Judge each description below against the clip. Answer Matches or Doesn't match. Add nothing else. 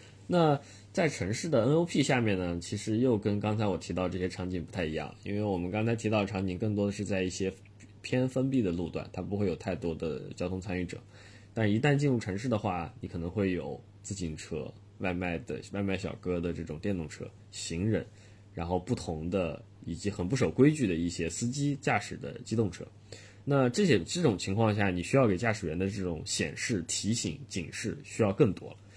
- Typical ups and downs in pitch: Matches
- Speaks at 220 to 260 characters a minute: Doesn't match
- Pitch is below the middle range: Matches